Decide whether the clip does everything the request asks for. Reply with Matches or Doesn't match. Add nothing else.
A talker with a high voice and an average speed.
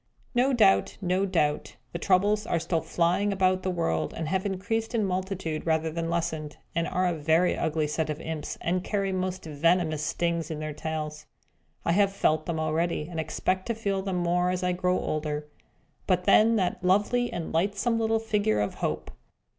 Doesn't match